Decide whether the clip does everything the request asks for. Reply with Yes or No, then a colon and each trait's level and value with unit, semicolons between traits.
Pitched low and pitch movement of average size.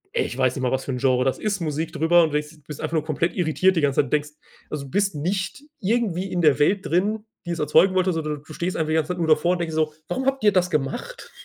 No: medium, 160 Hz; average, 3.8 semitones